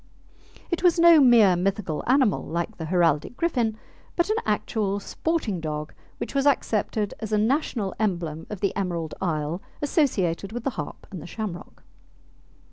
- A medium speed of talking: Yes, average, 155 wpm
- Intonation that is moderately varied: No, wide, 6.7 semitones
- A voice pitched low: No, high, 205 Hz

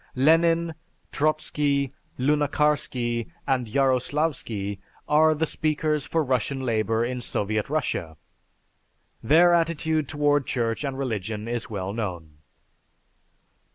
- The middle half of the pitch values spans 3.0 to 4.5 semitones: No, average, 5.0 semitones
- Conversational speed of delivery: No, slow, 100 wpm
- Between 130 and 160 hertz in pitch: Yes, low, 135 Hz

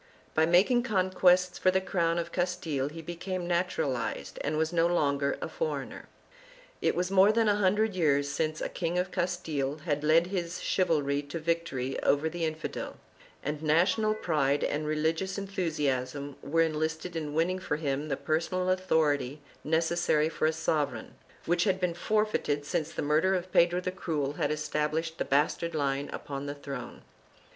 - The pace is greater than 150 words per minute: Yes, average, 170 wpm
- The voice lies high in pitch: No, medium, 165 Hz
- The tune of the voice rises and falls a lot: No, average, 3.5 semitones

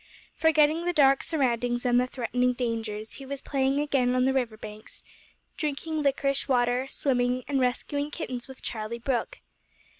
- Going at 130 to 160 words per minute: Yes, average, 155 wpm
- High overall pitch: Yes, very high, 255 Hz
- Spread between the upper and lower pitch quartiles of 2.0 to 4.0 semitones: Yes, narrow, 2.5 semitones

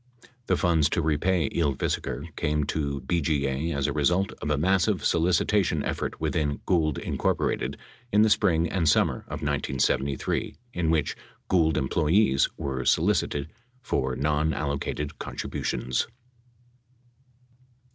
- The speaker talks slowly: Yes, slow, 120 wpm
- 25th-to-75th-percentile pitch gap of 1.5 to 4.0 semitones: Yes, average, 3.1 semitones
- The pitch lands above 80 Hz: No, very low, 75 Hz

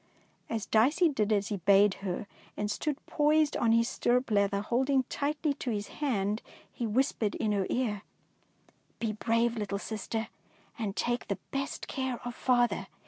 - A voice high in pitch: Yes, high, 230 Hz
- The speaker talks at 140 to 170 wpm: No, average, 185 wpm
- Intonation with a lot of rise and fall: No, average, 4.2 semitones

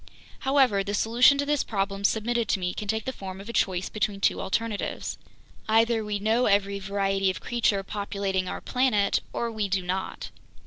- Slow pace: No, average, 185 wpm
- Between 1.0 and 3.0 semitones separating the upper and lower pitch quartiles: Yes, average, 2.7 semitones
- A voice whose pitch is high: Yes, high, 205 Hz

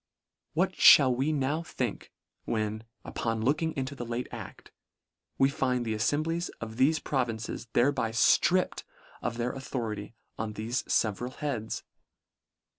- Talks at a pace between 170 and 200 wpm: No, slow, 135 wpm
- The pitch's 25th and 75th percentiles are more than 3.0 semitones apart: Yes, average, 3.6 semitones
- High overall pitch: No, low, 125 Hz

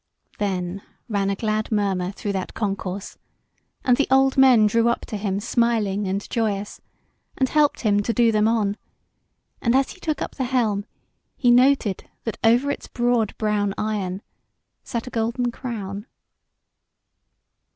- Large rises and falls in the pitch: No, average, 3.3 semitones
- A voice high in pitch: Yes, high, 215 Hz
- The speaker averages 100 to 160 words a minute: Yes, average, 150 wpm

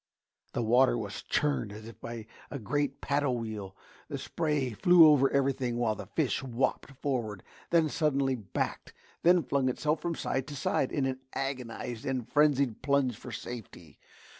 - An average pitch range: Yes, average, 3.6 semitones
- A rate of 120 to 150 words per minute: No, average, 165 wpm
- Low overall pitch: Yes, low, 130 Hz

